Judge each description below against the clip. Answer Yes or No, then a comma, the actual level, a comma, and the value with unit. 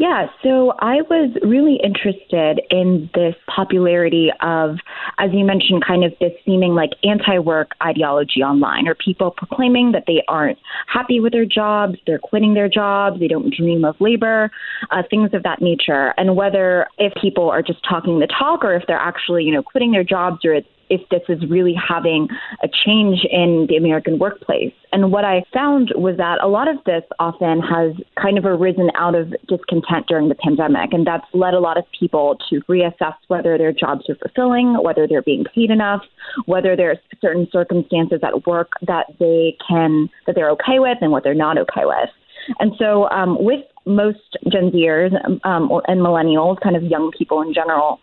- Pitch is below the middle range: No, medium, 180 Hz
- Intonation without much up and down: No, average, 3.5 semitones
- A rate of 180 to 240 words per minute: Yes, average, 190 wpm